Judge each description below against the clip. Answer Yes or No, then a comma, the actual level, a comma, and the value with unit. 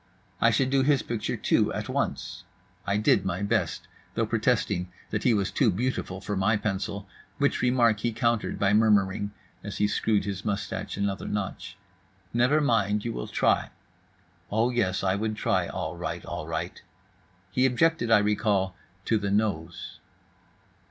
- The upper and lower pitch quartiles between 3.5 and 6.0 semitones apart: No, average, 3.0 semitones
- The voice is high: No, low, 105 Hz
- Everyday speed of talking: Yes, average, 160 wpm